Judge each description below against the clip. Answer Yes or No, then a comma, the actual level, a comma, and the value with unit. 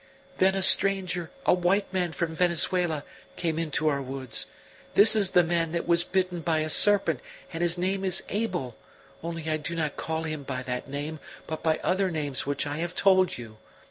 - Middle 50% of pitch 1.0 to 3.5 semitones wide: Yes, average, 3.2 semitones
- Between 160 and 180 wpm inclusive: No, average, 195 wpm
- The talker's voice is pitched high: No, medium, 165 Hz